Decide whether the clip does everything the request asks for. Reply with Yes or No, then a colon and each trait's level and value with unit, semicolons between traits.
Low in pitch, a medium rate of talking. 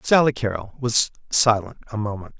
Yes: low, 115 Hz; average, 150 wpm